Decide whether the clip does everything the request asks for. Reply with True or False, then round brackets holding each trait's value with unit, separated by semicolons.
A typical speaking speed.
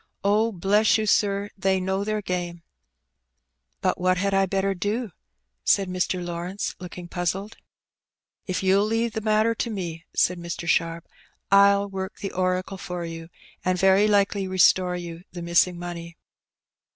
True (160 wpm)